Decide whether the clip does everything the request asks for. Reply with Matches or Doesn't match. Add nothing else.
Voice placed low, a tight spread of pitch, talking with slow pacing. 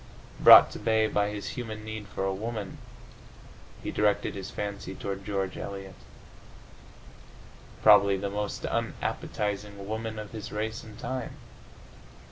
Matches